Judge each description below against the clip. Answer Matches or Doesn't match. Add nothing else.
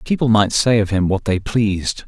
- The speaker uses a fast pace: Matches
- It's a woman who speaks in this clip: Doesn't match